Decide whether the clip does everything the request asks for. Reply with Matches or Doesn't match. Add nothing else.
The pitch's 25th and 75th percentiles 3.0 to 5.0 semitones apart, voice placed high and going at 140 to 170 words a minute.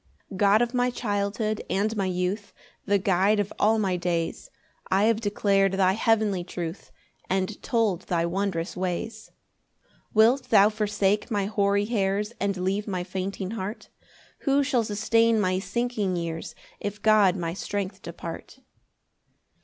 Doesn't match